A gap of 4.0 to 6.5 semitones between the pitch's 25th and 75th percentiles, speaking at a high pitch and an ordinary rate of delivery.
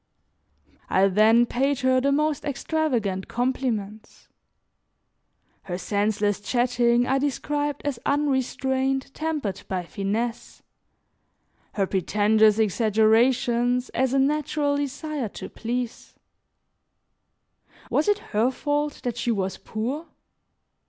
No: average, 4.5 semitones; high, 245 Hz; slow, 100 wpm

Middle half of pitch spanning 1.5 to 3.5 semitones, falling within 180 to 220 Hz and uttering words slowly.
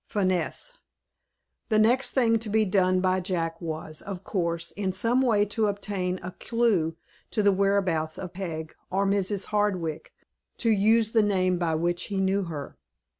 No: average, 3.2 semitones; high, 190 Hz; average, 165 wpm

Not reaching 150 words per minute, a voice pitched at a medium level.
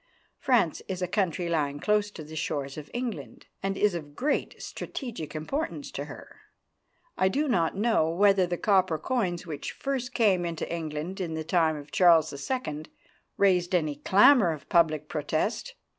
No: average, 165 wpm; medium, 175 Hz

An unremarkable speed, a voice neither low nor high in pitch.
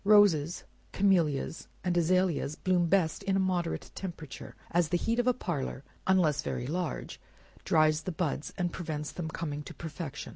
Yes: average, 160 wpm; medium, 170 Hz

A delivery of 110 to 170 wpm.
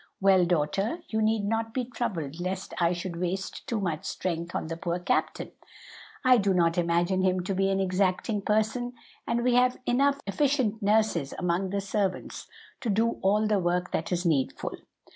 No: average, 180 wpm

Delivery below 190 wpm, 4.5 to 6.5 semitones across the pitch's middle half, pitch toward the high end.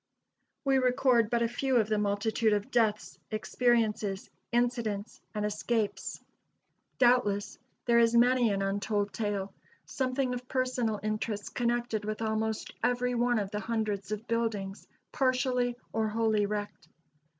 No: slow, 135 wpm; average, 2.7 semitones; high, 225 Hz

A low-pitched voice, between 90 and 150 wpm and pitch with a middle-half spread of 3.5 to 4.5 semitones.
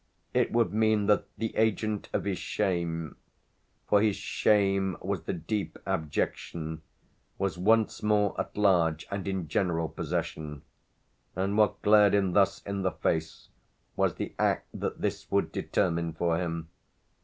Yes: very low, 95 Hz; average, 145 wpm; average, 3.8 semitones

